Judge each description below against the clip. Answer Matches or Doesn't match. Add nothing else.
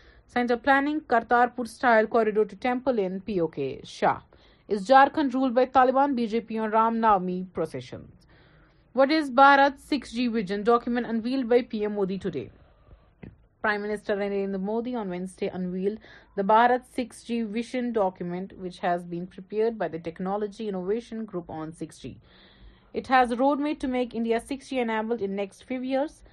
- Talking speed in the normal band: Matches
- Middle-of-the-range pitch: Doesn't match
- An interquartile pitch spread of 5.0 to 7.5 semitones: Doesn't match